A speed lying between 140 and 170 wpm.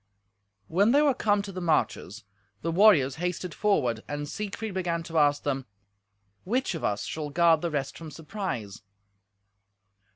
Yes: average, 155 wpm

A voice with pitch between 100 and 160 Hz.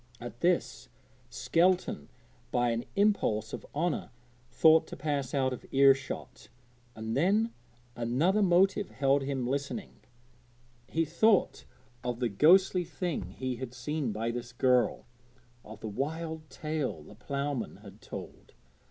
Yes: medium, 140 Hz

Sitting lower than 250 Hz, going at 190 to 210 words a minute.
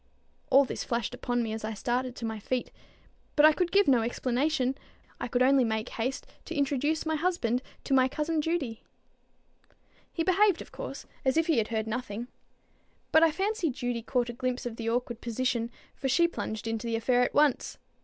No: very high, 255 Hz; average, 195 wpm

